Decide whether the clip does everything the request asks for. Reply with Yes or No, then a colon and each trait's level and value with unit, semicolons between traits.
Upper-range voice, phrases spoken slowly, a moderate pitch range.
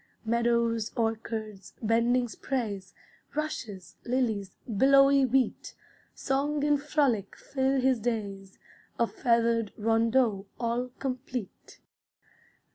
Yes: high, 235 Hz; slow, 90 wpm; average, 3.2 semitones